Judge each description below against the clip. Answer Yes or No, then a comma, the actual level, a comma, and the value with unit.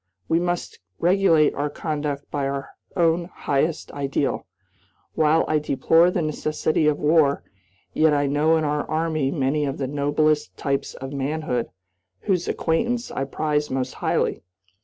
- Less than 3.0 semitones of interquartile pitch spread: Yes, narrow, 2.4 semitones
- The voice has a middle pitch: Yes, medium, 150 Hz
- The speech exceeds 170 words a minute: No, average, 145 wpm